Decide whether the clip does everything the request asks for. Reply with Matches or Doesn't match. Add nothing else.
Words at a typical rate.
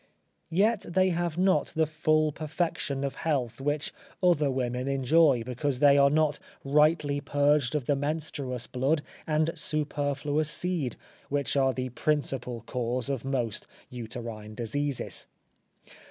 Doesn't match